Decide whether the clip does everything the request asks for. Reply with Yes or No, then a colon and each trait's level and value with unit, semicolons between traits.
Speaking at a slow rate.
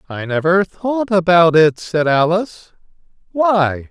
Yes: slow, 125 wpm